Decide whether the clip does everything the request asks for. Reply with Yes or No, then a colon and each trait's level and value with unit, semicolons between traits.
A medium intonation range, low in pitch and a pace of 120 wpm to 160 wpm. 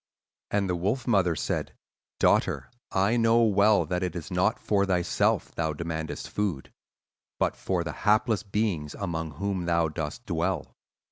Yes: average, 3.8 semitones; very low, 95 Hz; average, 150 wpm